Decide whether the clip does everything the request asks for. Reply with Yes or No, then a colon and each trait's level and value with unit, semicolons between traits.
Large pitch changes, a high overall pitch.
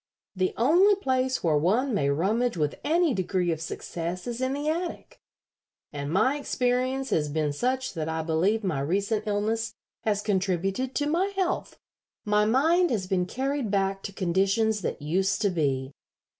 Yes: wide, 6.8 semitones; high, 205 Hz